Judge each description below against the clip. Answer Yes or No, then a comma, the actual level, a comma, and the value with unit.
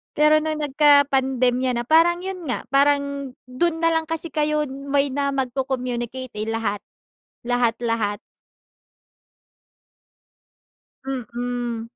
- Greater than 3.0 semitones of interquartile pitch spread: Yes, average, 3.6 semitones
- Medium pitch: No, very high, 270 Hz